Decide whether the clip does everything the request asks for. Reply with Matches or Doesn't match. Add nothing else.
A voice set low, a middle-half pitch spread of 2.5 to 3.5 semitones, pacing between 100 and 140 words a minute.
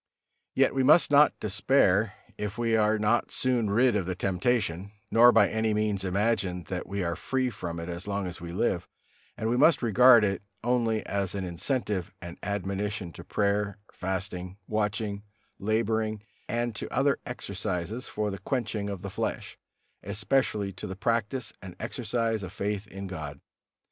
Doesn't match